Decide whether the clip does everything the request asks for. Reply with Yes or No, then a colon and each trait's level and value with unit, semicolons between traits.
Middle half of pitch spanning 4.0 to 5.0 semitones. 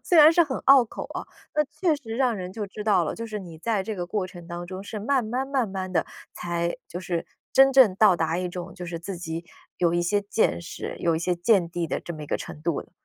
Yes: average, 4.7 semitones